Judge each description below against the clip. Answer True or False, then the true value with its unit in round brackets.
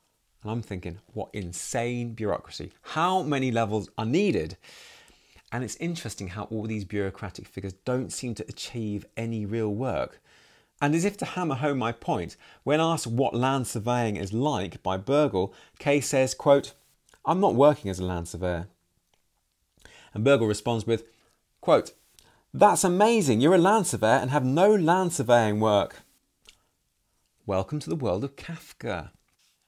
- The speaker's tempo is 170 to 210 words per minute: False (155 wpm)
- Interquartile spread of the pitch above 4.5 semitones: True (5.5 semitones)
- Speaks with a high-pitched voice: False (120 Hz)